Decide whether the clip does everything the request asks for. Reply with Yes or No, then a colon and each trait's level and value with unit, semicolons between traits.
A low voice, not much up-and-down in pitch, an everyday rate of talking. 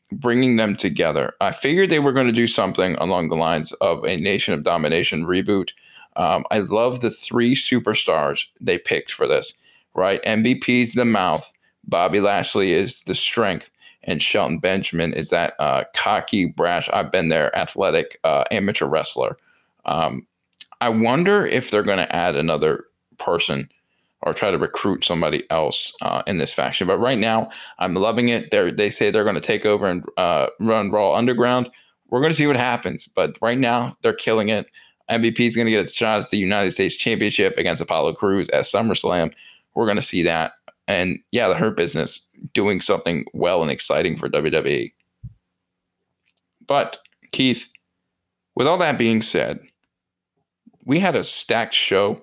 No: low, 115 Hz; average, 3.8 semitones; average, 175 wpm